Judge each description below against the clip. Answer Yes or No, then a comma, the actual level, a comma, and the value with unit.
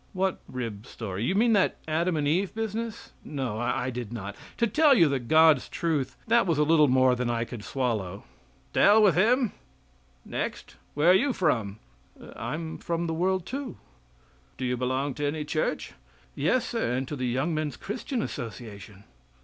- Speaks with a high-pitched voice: No, medium, 150 Hz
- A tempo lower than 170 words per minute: No, average, 180 wpm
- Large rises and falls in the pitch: Yes, wide, 7.3 semitones